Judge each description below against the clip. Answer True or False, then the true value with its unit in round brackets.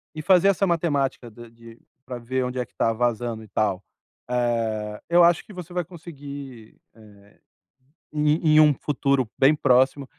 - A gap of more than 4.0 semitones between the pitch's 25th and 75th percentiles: True (4.8 semitones)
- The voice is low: True (130 Hz)